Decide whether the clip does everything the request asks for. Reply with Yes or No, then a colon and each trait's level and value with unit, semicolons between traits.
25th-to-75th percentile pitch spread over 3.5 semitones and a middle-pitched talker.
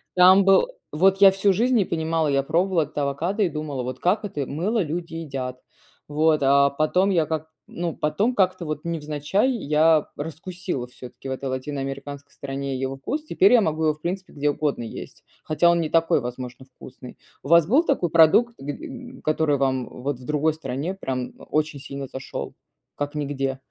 Yes: average, 4.7 semitones; medium, 155 Hz